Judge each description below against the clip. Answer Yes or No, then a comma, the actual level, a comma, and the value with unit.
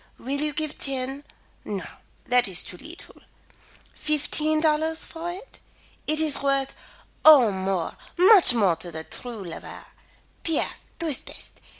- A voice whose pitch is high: Yes, very high, 280 Hz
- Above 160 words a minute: No, average, 140 wpm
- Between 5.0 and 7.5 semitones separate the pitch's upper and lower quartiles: Yes, wide, 5.6 semitones